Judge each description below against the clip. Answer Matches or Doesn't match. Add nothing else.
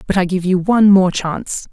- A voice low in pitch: Doesn't match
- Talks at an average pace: Doesn't match